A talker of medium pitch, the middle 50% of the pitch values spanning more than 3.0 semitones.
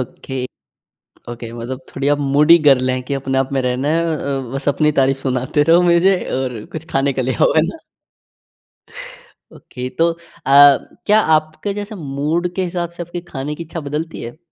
Yes: medium, 145 Hz; average, 3.9 semitones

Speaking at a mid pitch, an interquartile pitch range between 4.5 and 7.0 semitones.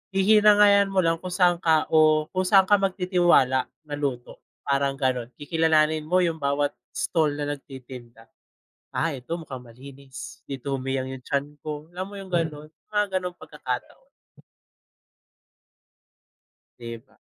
Yes: medium, 155 Hz; average, 5.0 semitones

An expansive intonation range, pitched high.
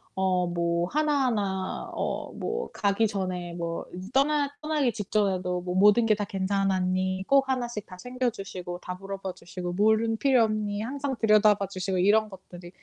No: average, 3.8 semitones; high, 200 Hz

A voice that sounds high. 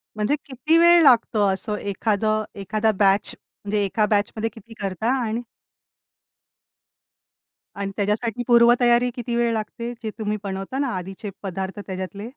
Yes: high, 215 Hz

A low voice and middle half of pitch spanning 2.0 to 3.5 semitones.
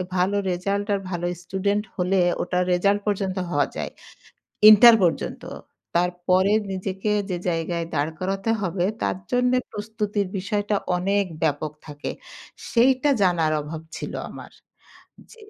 No: high, 190 Hz; narrow, 2.6 semitones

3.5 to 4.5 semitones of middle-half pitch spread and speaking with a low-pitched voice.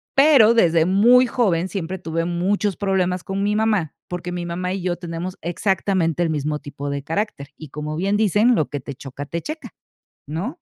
No: average, 4.0 semitones; medium, 180 Hz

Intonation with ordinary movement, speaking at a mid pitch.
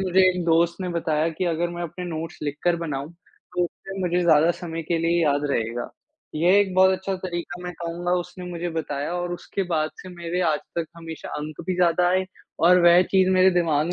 No: narrow, 1.7 semitones; medium, 170 Hz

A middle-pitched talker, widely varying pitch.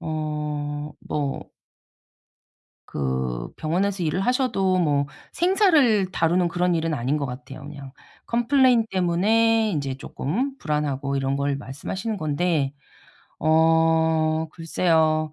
No: medium, 160 Hz; average, 4.8 semitones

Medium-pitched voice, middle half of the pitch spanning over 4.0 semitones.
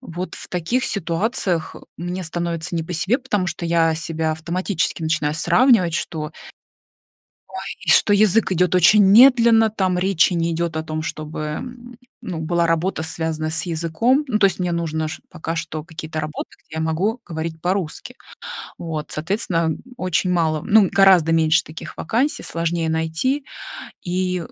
No: medium, 170 Hz; average, 3.3 semitones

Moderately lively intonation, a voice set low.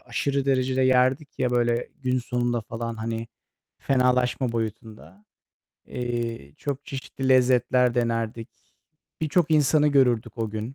No: narrow, 2.3 semitones; low, 125 Hz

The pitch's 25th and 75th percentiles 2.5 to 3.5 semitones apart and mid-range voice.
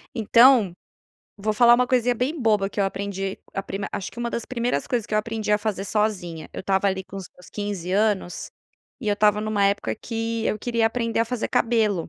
No: average, 2.8 semitones; high, 215 Hz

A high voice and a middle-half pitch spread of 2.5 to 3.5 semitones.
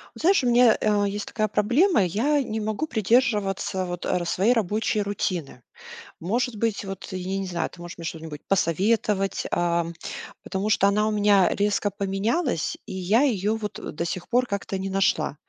Yes: high, 205 Hz; average, 3.0 semitones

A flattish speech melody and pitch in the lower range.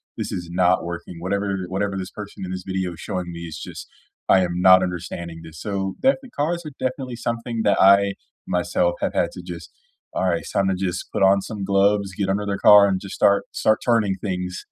Yes: narrow, 2.1 semitones; very low, 95 Hz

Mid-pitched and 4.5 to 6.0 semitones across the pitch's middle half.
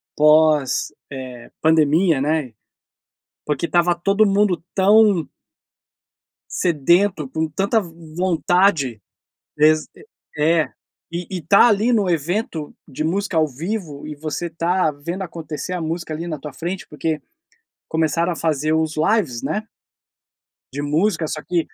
No: medium, 165 Hz; average, 3.3 semitones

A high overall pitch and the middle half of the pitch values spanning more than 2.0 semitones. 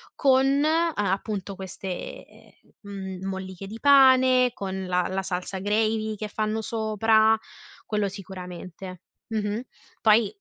Yes: high, 210 Hz; average, 2.8 semitones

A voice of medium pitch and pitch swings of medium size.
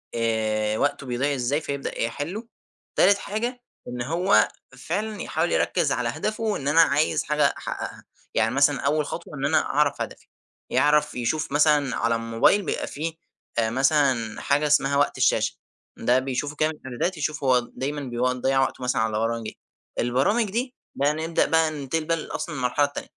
Yes: medium, 145 Hz; average, 4.1 semitones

